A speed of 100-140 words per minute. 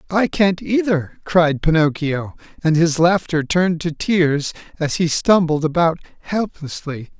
Yes: slow, 135 wpm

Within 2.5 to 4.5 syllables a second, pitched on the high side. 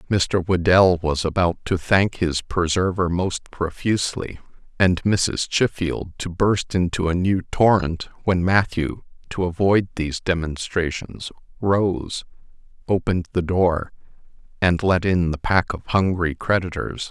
No: 4.1 syllables/s; very low, 90 Hz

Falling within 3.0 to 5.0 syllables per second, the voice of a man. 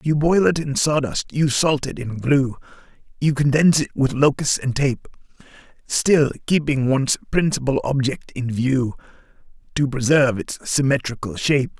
Yes: 4.8 syllables/s; male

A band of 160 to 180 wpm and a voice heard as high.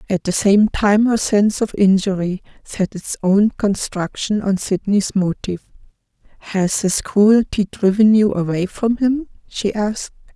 No: average, 145 wpm; high, 205 Hz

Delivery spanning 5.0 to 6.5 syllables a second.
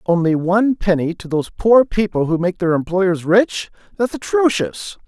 No: 4.8 syllables/s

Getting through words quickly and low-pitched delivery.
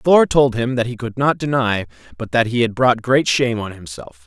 Yes: fast, 240 wpm; low, 125 Hz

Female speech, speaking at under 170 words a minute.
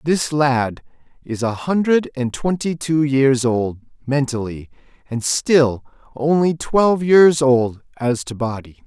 No: male; slow, 135 wpm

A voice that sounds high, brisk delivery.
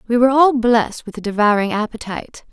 No: high, 230 Hz; average, 190 wpm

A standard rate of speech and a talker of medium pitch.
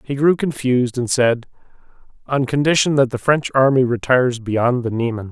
No: average, 170 wpm; low, 130 Hz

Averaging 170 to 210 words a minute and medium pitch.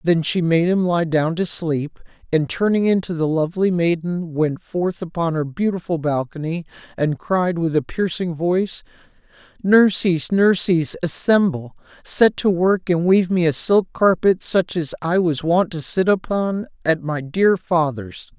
No: average, 160 wpm; medium, 170 Hz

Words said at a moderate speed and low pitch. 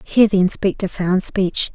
No: average, 170 wpm; high, 190 Hz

